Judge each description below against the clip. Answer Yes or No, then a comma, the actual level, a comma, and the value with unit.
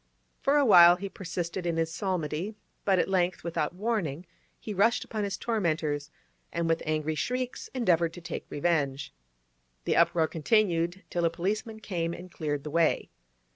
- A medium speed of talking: Yes, average, 165 wpm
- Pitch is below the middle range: No, medium, 175 Hz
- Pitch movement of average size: Yes, average, 3.5 semitones